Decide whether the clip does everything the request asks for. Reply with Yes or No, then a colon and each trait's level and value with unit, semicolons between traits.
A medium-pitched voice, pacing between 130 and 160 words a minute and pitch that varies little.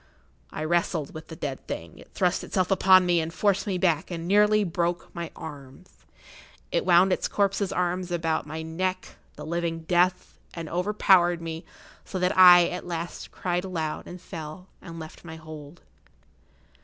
No: medium, 175 Hz; average, 170 wpm; narrow, 2.3 semitones